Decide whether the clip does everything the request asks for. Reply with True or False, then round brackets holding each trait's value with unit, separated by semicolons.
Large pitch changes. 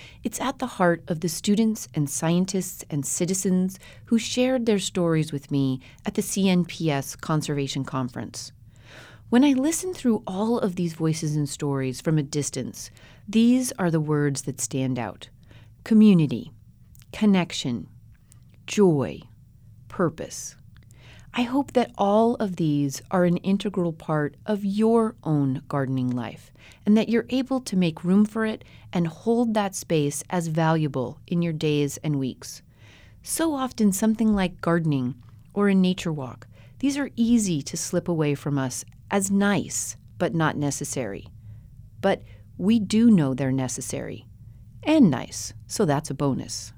True (7.7 semitones)